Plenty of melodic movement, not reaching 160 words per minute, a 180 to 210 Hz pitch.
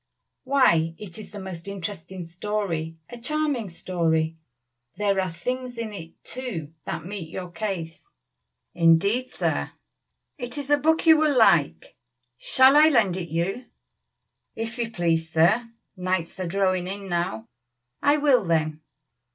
Yes: wide, 6.3 semitones; average, 145 wpm; high, 190 Hz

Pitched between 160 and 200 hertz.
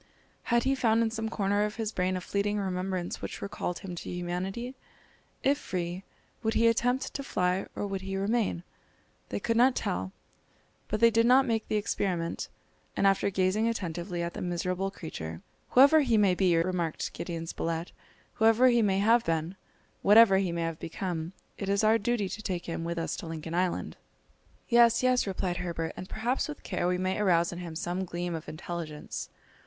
Yes: high, 190 Hz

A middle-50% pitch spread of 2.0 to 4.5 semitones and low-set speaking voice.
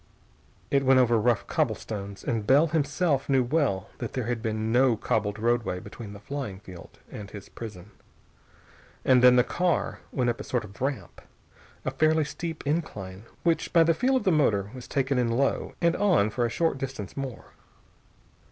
No: average, 5.1 semitones; low, 125 Hz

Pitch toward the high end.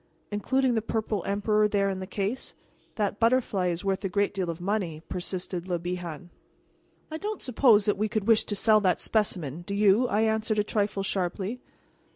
Yes: high, 205 Hz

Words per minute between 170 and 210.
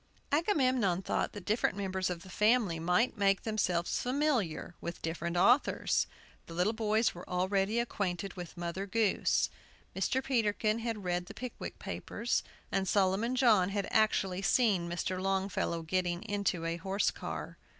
No: average, 150 wpm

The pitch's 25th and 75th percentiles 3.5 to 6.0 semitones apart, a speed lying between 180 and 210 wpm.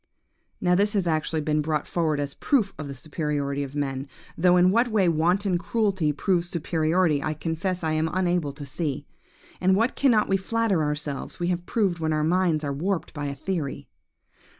Yes: average, 3.9 semitones; average, 195 wpm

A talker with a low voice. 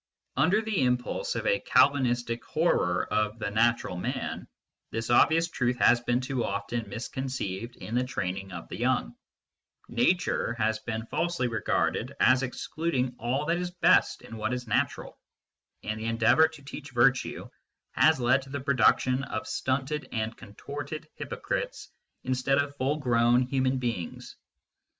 Yes: low, 125 Hz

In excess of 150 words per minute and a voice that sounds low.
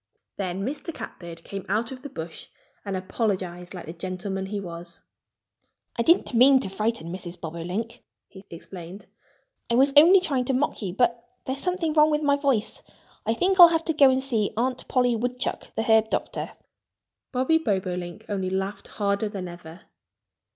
No: average, 170 wpm; high, 215 Hz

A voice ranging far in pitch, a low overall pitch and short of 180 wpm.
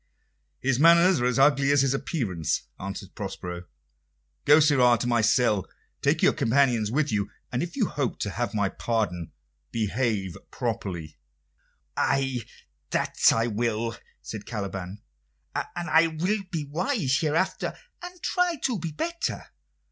Yes: wide, 6.8 semitones; low, 125 Hz; average, 140 wpm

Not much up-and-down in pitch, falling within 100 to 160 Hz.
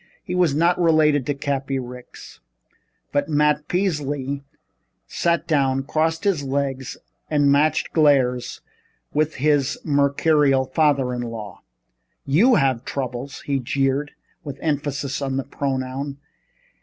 Yes: narrow, 2.2 semitones; medium, 140 Hz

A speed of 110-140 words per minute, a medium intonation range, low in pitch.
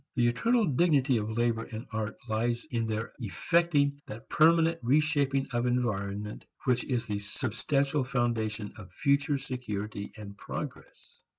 Yes: slow, 135 wpm; average, 4.5 semitones; low, 120 Hz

